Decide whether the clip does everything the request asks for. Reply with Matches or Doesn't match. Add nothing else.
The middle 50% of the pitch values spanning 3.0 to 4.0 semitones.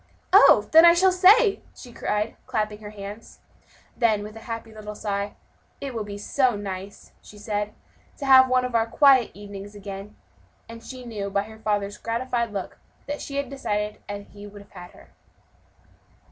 Matches